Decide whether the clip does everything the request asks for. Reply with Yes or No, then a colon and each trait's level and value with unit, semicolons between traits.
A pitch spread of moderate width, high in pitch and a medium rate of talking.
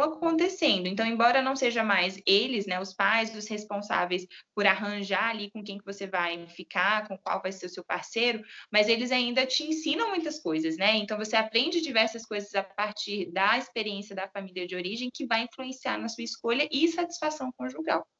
No: average, 4.7 semitones; high, 215 Hz; fast, 190 wpm